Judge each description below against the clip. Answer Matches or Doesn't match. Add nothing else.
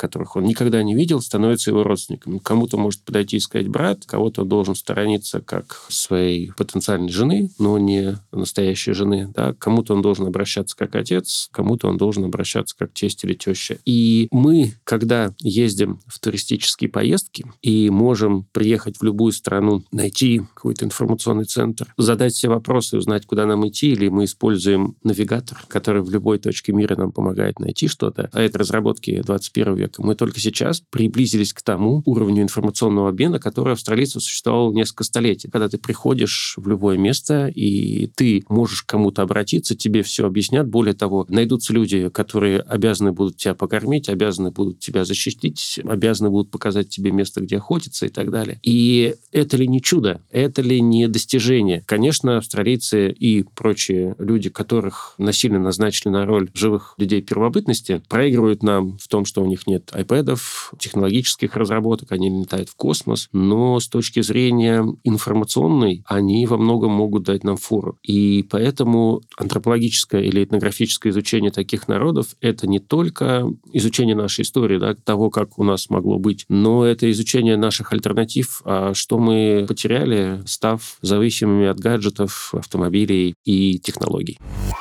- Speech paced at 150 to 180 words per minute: Matches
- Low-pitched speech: Matches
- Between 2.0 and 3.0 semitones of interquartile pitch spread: Matches